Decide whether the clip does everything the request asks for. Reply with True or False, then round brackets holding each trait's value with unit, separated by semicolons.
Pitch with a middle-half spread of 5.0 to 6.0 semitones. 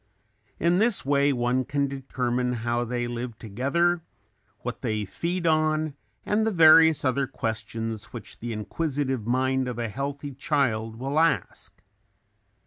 False (4.6 semitones)